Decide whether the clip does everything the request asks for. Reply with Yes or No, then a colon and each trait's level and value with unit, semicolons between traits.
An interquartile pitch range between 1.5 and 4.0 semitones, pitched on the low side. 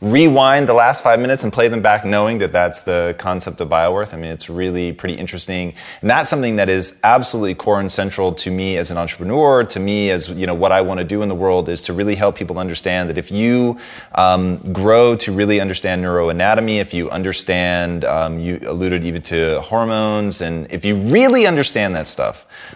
Yes: average, 2.9 semitones; very low, 95 Hz